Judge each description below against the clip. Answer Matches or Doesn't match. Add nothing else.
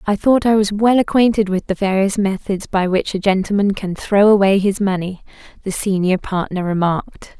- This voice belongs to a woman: Matches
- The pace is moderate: Matches